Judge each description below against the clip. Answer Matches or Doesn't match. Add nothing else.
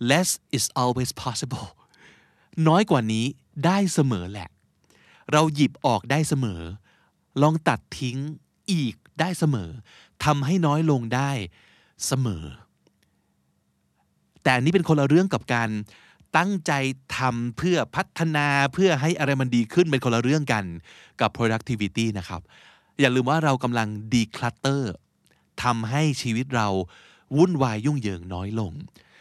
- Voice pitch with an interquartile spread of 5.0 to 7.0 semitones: Matches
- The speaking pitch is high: Doesn't match